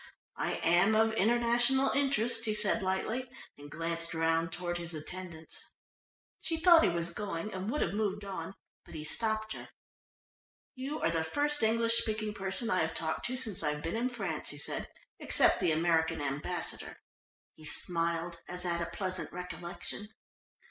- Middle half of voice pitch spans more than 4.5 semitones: Yes, average, 5.2 semitones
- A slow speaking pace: No, average, 165 wpm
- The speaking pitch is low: No, medium, 185 Hz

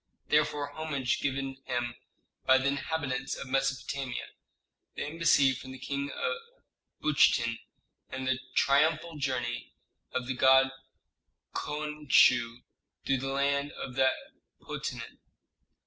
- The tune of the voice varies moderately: No, narrow, 1.7 semitones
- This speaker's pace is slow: Yes, slow, 115 wpm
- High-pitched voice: No, low, 135 Hz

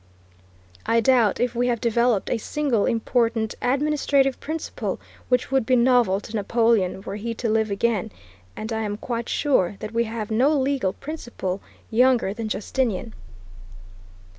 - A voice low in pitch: No, high, 230 Hz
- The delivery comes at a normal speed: Yes, average, 150 wpm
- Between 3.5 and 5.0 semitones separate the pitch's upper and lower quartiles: No, average, 2.8 semitones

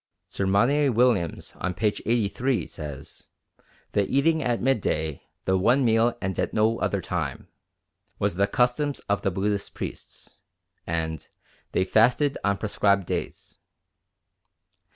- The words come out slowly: Yes, slow, 130 wpm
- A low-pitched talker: Yes, low, 105 Hz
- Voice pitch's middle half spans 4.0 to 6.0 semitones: Yes, average, 4.6 semitones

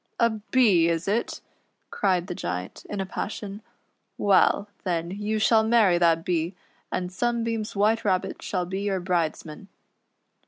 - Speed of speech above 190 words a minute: No, average, 145 wpm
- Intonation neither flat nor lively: Yes, average, 3.6 semitones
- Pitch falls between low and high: No, high, 195 Hz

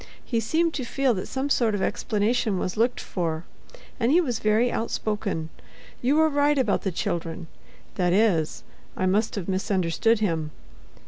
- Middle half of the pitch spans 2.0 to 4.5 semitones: No, average, 4.9 semitones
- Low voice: No, high, 215 Hz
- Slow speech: No, average, 155 wpm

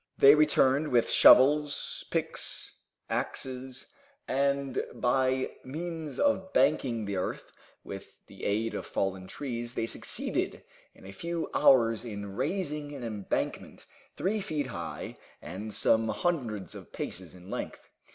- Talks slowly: Yes, slow, 130 wpm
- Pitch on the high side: No, low, 130 Hz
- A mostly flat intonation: No, average, 5.3 semitones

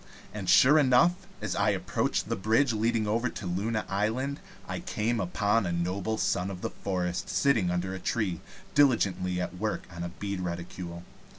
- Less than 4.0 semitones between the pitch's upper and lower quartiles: No, average, 4.3 semitones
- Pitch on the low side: Yes, low, 100 Hz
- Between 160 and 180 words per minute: Yes, average, 175 wpm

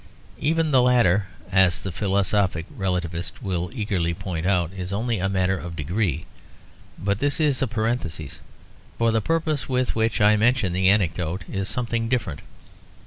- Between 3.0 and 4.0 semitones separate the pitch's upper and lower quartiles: No, average, 4.6 semitones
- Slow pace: No, average, 155 wpm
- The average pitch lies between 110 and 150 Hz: No, low, 100 Hz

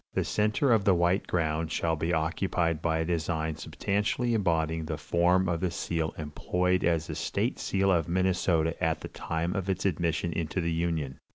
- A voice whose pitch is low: Yes, very low, 85 Hz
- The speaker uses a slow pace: No, average, 185 wpm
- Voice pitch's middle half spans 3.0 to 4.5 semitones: No, narrow, 2.4 semitones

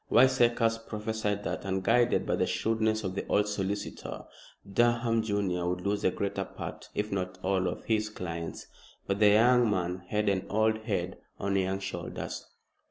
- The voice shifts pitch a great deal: No, narrow, 2.6 semitones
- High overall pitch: No, low, 105 Hz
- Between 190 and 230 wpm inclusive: No, average, 165 wpm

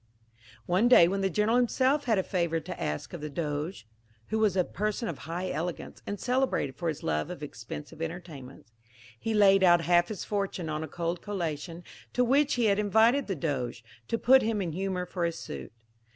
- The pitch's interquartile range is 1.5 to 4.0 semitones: No, average, 4.9 semitones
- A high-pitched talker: No, medium, 180 Hz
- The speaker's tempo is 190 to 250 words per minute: Yes, average, 200 wpm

